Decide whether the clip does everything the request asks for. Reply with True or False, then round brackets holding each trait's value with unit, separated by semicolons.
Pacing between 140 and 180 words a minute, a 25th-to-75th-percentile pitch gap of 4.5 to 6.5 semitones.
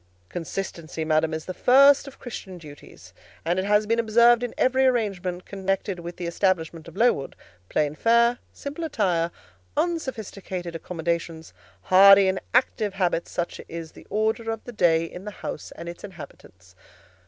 True (155 wpm; 5.1 semitones)